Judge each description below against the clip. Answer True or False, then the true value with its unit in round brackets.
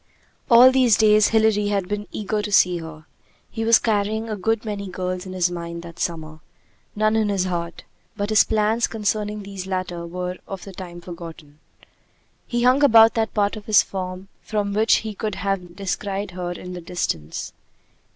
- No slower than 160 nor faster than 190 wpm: True (180 wpm)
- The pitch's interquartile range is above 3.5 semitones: False (3.1 semitones)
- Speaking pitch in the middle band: False (200 Hz)